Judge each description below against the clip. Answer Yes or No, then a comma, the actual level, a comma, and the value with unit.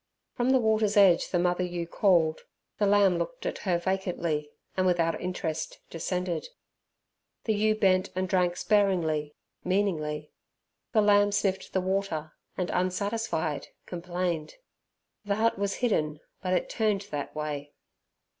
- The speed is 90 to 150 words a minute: Yes, slow, 135 wpm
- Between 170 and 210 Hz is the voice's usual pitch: Yes, medium, 185 Hz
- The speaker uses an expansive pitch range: No, average, 3.4 semitones